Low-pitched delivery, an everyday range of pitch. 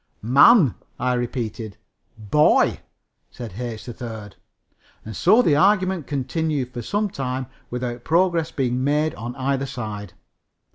Yes: low, 130 Hz; average, 4.7 semitones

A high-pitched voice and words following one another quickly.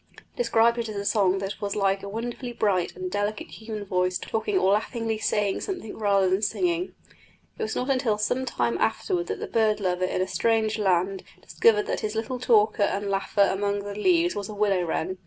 Yes: high, 210 Hz; fast, 210 wpm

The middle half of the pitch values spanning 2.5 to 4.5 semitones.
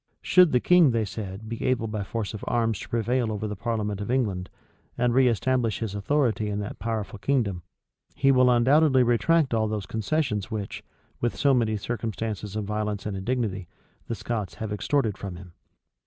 Yes: average, 3.2 semitones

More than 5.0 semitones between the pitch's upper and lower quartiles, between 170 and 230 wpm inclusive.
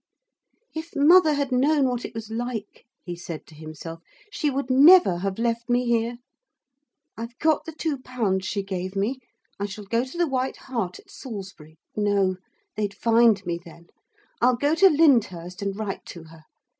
Yes: wide, 5.6 semitones; average, 175 wpm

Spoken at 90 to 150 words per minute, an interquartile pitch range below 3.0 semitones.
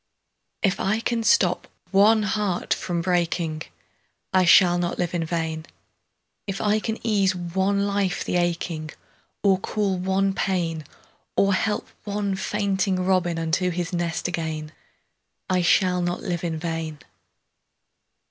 Yes: average, 140 wpm; narrow, 2.6 semitones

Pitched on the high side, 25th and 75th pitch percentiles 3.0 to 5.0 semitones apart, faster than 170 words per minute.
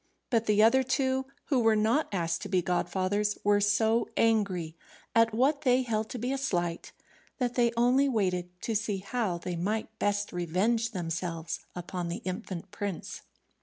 No: high, 210 Hz; average, 4.6 semitones; average, 165 wpm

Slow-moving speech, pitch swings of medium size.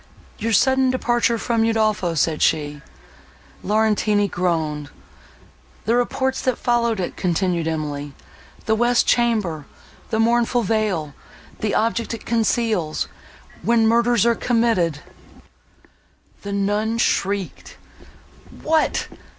Yes: slow, 90 wpm; average, 5.0 semitones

